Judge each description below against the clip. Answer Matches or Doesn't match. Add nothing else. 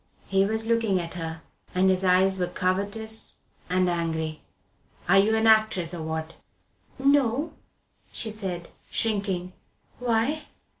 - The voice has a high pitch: Matches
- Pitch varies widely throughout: Doesn't match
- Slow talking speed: Matches